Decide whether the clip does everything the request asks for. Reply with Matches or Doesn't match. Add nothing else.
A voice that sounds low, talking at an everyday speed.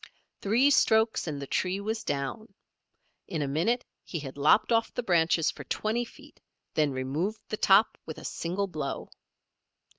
Doesn't match